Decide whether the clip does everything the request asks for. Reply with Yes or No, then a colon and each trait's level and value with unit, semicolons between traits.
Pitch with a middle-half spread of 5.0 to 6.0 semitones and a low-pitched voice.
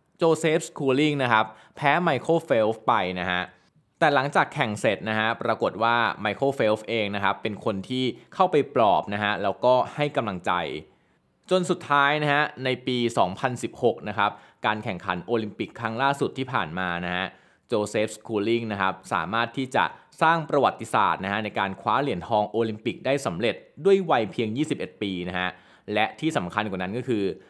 Yes: wide, 5.6 semitones; low, 115 Hz